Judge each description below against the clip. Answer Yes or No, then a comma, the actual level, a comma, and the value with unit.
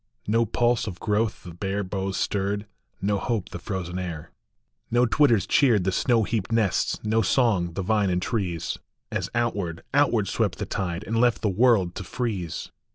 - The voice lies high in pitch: No, low, 100 Hz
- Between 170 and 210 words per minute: Yes, average, 175 wpm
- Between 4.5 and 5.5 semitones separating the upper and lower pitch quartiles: No, average, 3.8 semitones